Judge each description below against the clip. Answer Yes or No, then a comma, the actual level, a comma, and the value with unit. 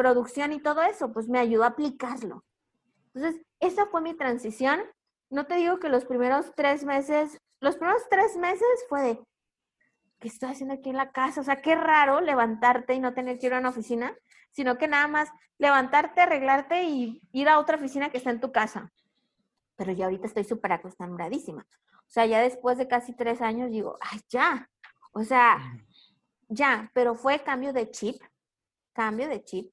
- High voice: Yes, very high, 260 Hz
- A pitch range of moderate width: Yes, average, 3.9 semitones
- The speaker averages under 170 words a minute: No, average, 185 wpm